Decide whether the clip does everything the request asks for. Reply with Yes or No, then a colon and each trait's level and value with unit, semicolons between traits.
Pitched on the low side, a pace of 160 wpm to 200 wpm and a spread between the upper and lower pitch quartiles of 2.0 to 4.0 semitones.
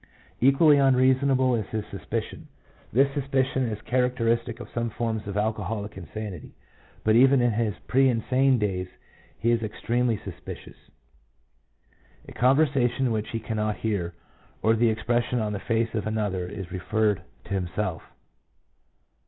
No: low, 115 Hz; average, 140 wpm; average, 3.1 semitones